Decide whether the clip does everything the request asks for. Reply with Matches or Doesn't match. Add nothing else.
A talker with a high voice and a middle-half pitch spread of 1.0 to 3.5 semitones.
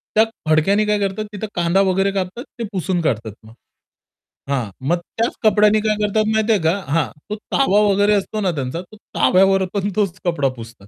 Doesn't match